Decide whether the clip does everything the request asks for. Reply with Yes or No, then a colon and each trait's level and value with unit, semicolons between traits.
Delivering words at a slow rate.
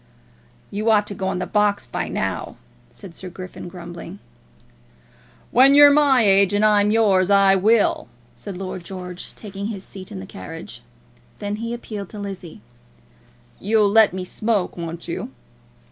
No: average, 155 wpm